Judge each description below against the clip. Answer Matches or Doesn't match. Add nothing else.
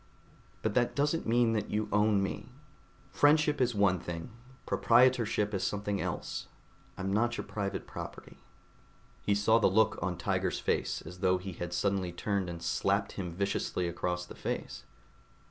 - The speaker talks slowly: Doesn't match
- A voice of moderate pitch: Doesn't match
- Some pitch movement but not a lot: Matches